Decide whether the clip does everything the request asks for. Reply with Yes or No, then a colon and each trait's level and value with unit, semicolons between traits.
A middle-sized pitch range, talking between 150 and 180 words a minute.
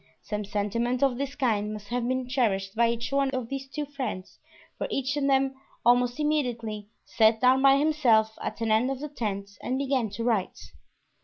No: average, 3.7 semitones; average, 190 wpm